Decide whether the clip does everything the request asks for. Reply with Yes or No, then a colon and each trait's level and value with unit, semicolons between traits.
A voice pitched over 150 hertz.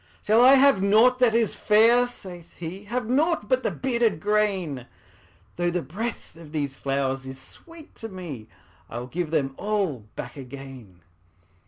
Yes: high, 190 Hz